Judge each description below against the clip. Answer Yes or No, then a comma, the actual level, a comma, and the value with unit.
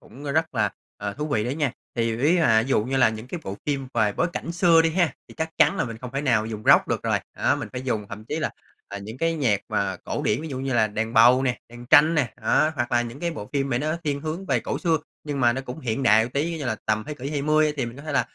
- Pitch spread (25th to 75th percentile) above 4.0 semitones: Yes, average, 4.9 semitones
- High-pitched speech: No, low, 130 Hz